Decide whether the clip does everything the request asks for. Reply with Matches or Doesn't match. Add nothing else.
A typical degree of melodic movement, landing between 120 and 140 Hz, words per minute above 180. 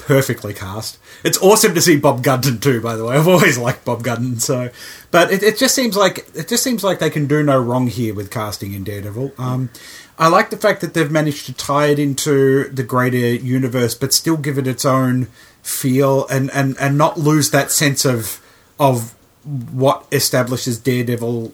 Matches